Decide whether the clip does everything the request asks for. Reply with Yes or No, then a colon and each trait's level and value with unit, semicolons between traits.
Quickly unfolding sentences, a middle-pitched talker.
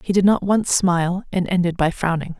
Yes: fast, 225 wpm; medium, 180 Hz